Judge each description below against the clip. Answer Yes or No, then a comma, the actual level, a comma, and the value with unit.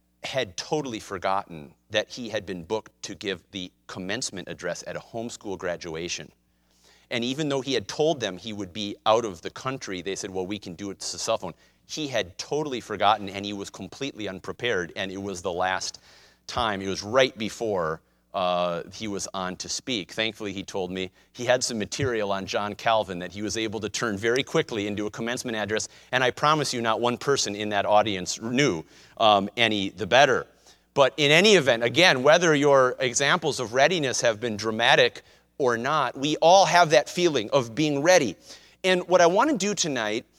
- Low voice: Yes, low, 105 Hz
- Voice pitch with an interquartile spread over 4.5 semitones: Yes, average, 5.0 semitones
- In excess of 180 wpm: Yes, average, 200 wpm